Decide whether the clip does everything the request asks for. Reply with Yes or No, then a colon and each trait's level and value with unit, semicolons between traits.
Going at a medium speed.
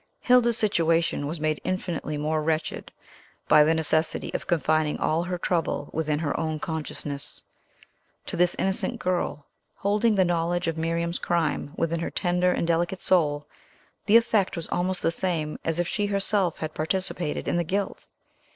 Yes: average, 160 wpm